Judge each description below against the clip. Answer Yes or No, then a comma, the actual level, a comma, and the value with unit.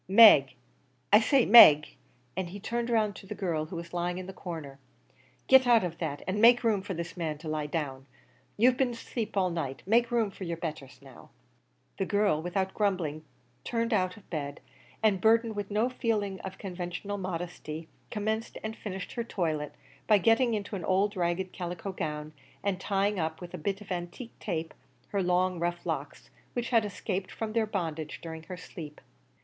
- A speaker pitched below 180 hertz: No, high, 190 Hz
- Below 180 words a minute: No, average, 190 wpm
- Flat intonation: No, average, 4.3 semitones